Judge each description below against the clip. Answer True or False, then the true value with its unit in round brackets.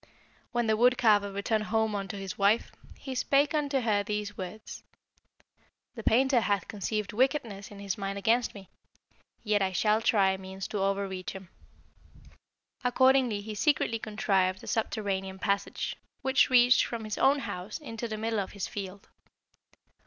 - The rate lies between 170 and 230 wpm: False (155 wpm)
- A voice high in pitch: True (210 Hz)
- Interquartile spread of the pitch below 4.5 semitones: True (3.1 semitones)